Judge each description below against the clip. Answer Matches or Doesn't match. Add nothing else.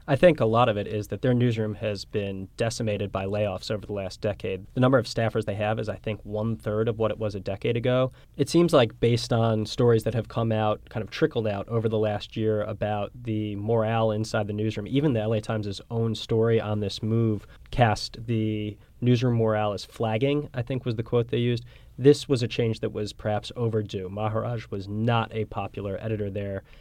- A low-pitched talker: Matches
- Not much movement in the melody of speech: Matches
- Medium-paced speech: Doesn't match